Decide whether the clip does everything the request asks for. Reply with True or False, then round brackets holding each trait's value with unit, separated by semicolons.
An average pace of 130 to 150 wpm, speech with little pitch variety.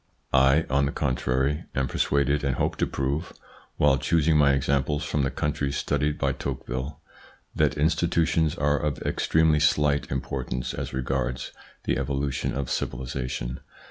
True (145 wpm; 1.9 semitones)